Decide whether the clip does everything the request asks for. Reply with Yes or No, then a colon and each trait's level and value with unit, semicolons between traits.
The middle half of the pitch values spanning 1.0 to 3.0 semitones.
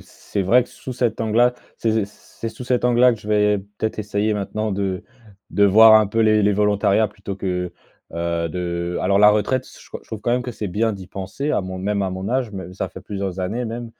Yes: average, 2.7 semitones